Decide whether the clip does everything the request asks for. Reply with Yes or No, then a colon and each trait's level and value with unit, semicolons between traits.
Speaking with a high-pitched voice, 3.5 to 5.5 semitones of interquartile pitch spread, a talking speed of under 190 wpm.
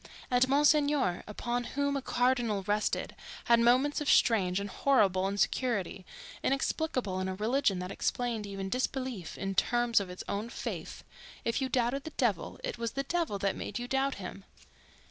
Yes: high, 235 Hz; average, 5.1 semitones; average, 165 wpm